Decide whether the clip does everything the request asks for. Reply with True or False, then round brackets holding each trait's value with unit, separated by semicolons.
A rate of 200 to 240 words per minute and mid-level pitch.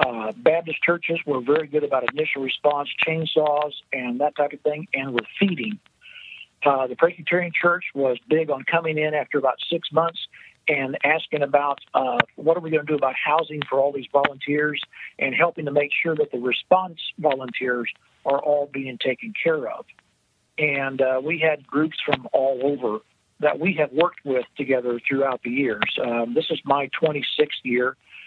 False (180 wpm; 145 Hz)